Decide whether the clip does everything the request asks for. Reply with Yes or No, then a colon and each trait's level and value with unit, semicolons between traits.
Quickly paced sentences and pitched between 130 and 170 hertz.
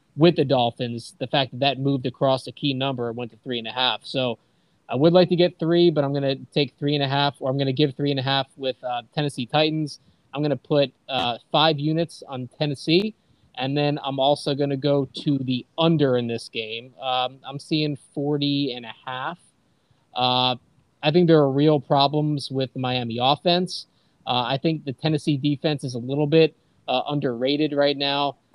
Yes: fast, 215 wpm; medium, 140 Hz